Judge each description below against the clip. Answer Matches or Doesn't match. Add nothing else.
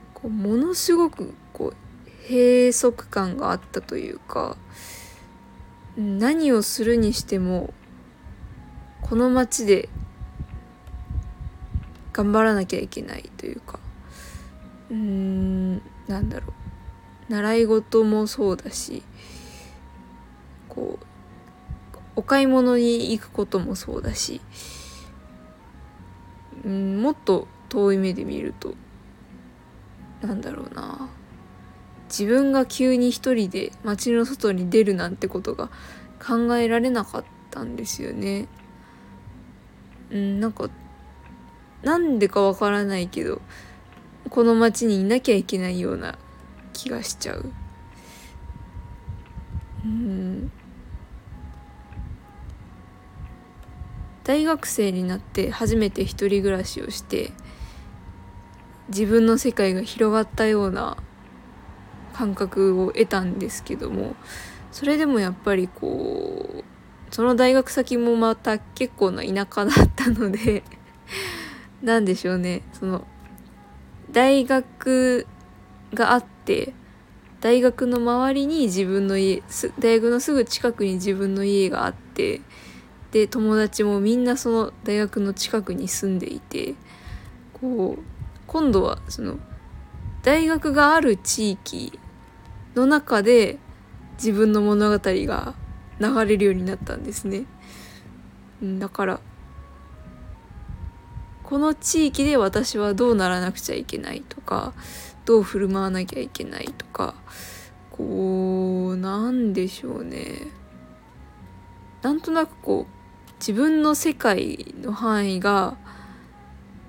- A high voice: Matches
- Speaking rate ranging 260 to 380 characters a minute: Doesn't match